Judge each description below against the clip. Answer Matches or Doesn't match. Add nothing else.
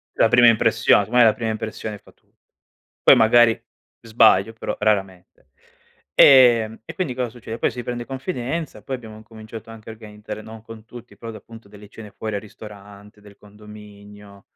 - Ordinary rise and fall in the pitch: Doesn't match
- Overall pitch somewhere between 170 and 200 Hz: Doesn't match